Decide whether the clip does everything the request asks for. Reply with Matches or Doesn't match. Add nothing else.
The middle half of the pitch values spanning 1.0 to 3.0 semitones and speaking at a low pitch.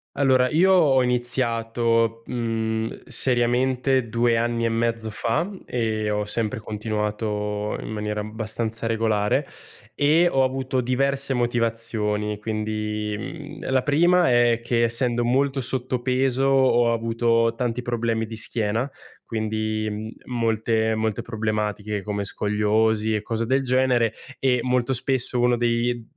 Matches